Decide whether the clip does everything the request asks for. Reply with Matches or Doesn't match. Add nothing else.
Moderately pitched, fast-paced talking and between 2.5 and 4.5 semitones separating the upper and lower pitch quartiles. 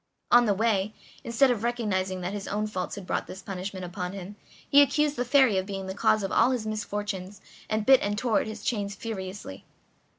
Doesn't match